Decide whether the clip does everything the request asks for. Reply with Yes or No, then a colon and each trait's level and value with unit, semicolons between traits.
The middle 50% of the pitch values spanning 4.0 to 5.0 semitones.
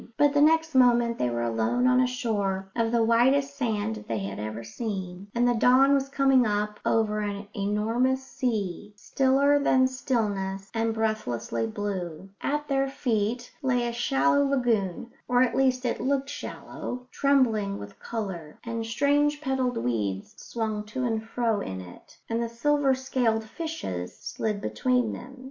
Yes: average, 4.4 semitones